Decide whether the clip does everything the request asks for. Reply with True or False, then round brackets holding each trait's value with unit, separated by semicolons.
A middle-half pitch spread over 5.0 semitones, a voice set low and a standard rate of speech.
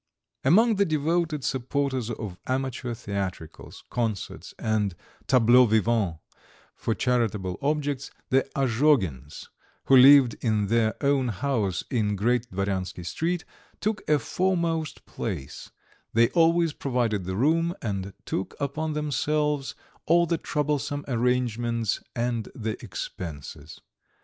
False (5.6 semitones; 125 Hz; 115 wpm)